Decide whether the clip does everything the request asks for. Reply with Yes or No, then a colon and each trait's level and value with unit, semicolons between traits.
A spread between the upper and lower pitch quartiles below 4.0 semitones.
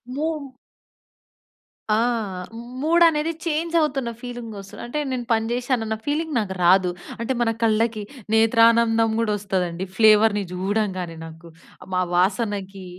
No: average, 4.4 semitones